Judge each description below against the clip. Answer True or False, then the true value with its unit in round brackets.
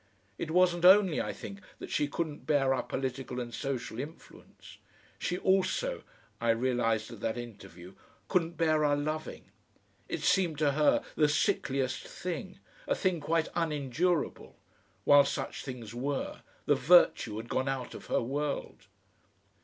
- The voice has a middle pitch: True (145 Hz)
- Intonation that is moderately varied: True (5.0 semitones)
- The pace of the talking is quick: False (145 wpm)